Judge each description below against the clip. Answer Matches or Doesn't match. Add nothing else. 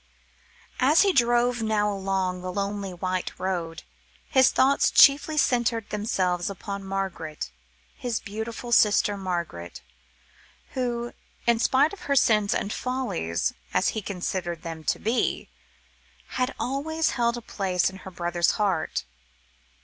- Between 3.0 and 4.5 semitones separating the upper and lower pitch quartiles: Doesn't match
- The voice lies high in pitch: Matches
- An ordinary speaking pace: Doesn't match